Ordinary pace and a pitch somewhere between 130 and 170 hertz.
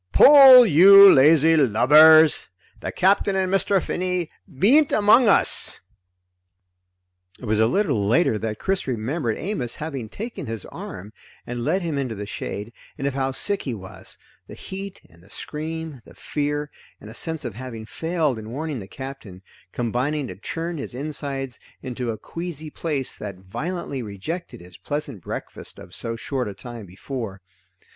Yes: average, 160 wpm; medium, 140 Hz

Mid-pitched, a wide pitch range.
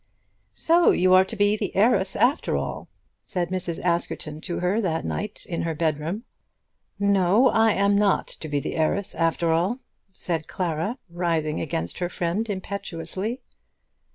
No: medium, 180 Hz; average, 3.7 semitones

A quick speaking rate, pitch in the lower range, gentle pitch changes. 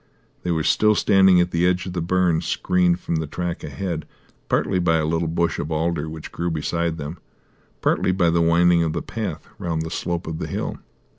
Yes: fast, 210 wpm; very low, 85 Hz; narrow, 1.7 semitones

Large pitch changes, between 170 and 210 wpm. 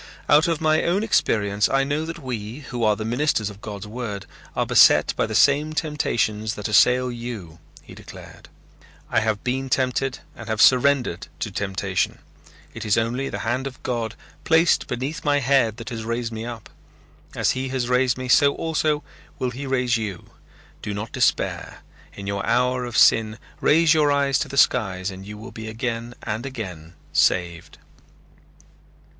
No: average, 4.1 semitones; average, 175 wpm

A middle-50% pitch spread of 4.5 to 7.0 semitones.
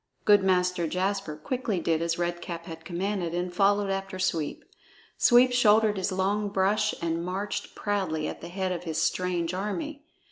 No: average, 3.1 semitones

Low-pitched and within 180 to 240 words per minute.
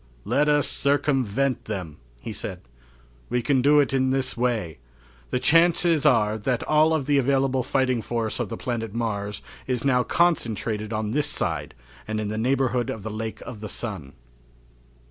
No: low, 125 Hz; average, 170 wpm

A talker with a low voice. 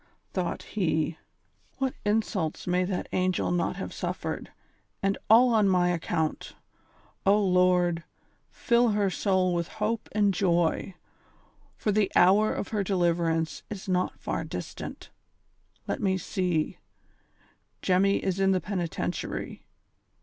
No: medium, 185 Hz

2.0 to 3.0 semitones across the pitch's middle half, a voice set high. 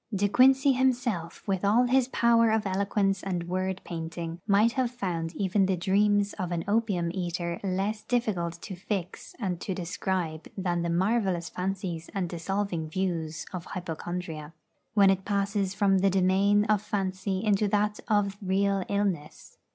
Yes: average, 2.7 semitones; high, 195 Hz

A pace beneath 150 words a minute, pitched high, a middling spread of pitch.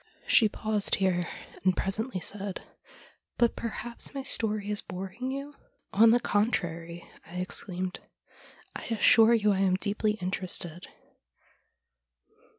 Yes: average, 140 wpm; high, 205 Hz; average, 3.5 semitones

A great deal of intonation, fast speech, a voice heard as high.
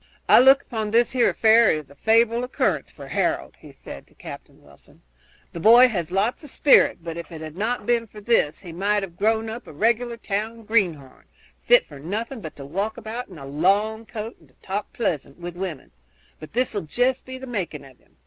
Yes: wide, 5.7 semitones; fast, 215 wpm; high, 210 Hz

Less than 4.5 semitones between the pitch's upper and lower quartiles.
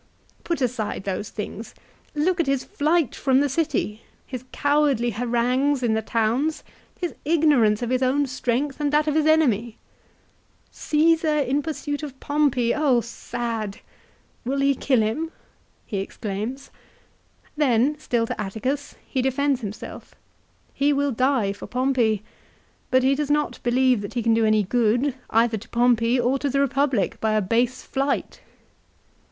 Yes: average, 3.9 semitones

